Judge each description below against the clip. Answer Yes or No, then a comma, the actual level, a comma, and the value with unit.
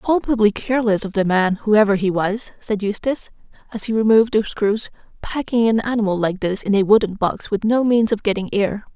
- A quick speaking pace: Yes, fast, 210 wpm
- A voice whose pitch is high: Yes, high, 210 Hz